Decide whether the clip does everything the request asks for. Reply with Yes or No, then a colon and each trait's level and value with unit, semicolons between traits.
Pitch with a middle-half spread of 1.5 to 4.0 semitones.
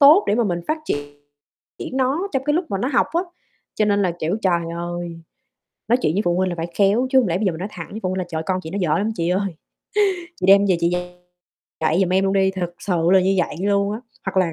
Yes: average, 3.4 semitones